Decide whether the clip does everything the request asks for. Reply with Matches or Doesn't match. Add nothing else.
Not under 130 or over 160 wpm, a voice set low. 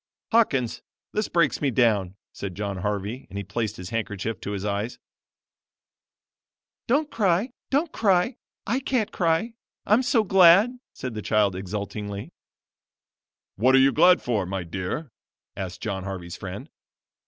Matches